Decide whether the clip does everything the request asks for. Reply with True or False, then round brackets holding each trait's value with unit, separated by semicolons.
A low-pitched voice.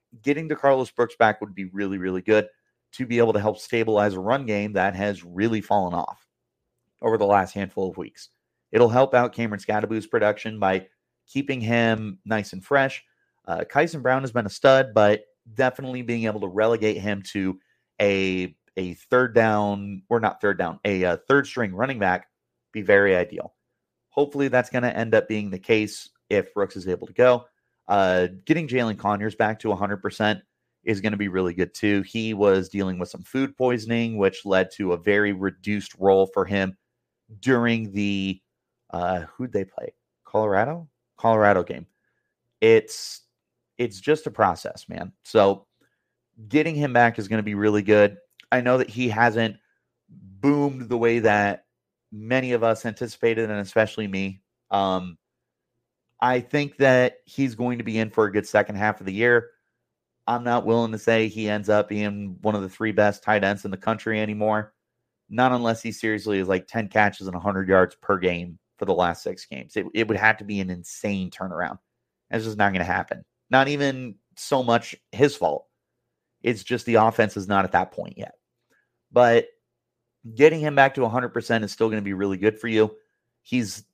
True (110 Hz)